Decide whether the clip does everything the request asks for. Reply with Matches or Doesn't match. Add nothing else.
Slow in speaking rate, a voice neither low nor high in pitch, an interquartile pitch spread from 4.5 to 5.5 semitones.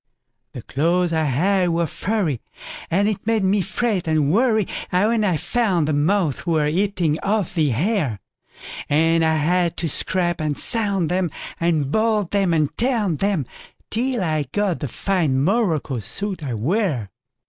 Doesn't match